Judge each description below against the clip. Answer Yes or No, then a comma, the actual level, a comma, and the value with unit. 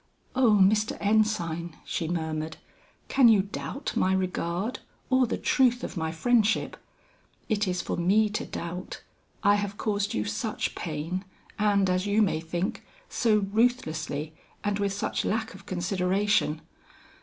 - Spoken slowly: No, average, 145 wpm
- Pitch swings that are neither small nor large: Yes, average, 3.9 semitones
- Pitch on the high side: Yes, high, 200 Hz